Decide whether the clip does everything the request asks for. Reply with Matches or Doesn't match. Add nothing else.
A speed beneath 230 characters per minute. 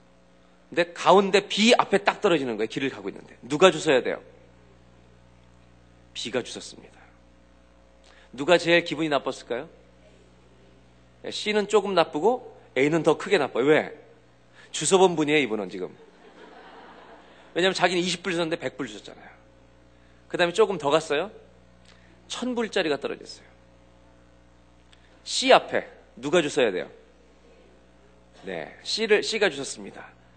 Doesn't match